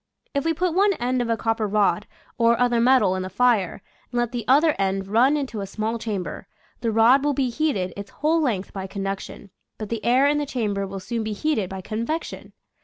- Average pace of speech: No, fast, 225 wpm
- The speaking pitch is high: Yes, high, 230 Hz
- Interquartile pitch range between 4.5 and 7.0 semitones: Yes, average, 4.9 semitones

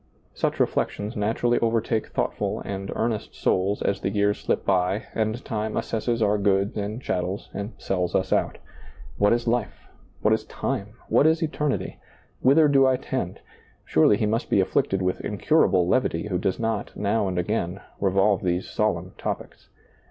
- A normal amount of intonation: Yes, average, 3.0 semitones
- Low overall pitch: Yes, low, 105 Hz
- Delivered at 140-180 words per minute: Yes, average, 165 wpm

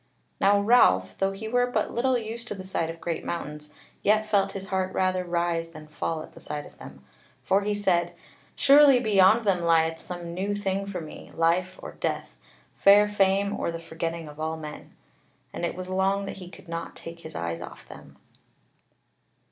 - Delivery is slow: No, average, 195 wpm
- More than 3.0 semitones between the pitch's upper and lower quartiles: Yes, average, 3.4 semitones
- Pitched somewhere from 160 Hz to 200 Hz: Yes, medium, 185 Hz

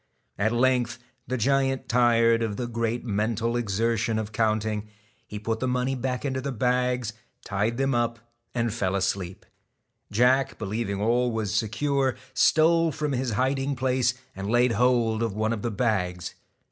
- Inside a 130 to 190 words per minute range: Yes, average, 160 wpm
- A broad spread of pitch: No, narrow, 2.6 semitones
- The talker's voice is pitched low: Yes, low, 115 Hz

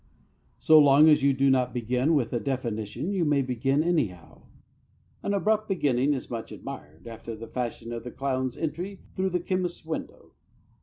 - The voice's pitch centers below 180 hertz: Yes, low, 135 Hz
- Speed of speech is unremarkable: Yes, average, 170 wpm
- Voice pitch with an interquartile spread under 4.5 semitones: No, average, 5.2 semitones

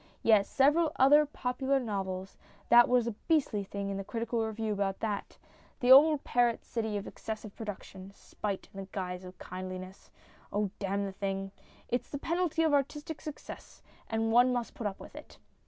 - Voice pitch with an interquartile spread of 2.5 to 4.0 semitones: No, average, 5.0 semitones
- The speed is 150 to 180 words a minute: Yes, average, 175 wpm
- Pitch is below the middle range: No, high, 220 Hz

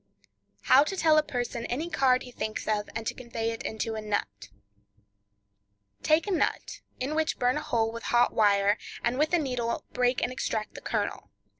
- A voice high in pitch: Yes, high, 230 Hz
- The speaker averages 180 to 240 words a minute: Yes, average, 190 wpm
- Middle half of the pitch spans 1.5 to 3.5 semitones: No, average, 4.3 semitones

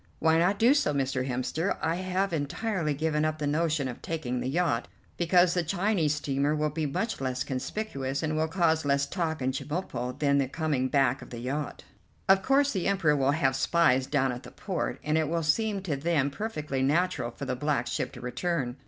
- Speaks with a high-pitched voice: No, medium, 150 Hz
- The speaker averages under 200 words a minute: No, fast, 205 wpm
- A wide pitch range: No, average, 4.3 semitones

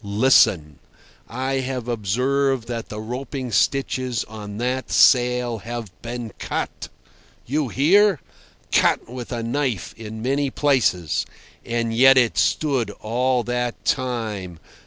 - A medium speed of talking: No, slow, 120 wpm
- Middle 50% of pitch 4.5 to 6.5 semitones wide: No, average, 2.9 semitones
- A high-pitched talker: No, low, 120 Hz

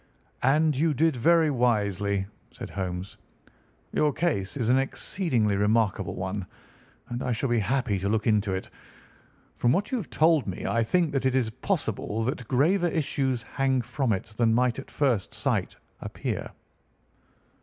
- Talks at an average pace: Yes, average, 160 wpm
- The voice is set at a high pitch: No, low, 125 Hz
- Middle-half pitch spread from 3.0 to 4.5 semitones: No, average, 5.3 semitones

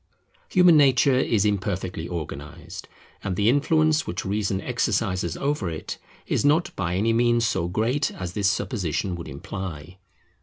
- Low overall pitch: Yes, low, 100 Hz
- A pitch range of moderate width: No, wide, 5.8 semitones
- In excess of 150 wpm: No, average, 145 wpm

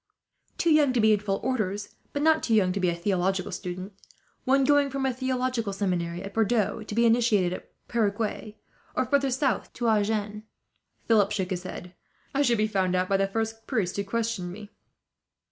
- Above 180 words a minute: Yes, average, 195 wpm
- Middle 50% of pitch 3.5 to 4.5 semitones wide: Yes, average, 3.9 semitones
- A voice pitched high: Yes, high, 215 Hz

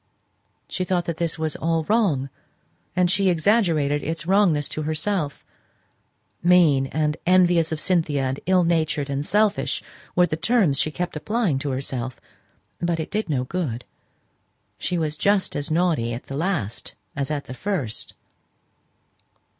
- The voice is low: No, medium, 160 Hz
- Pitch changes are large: No, average, 4.1 semitones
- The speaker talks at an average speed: Yes, average, 150 wpm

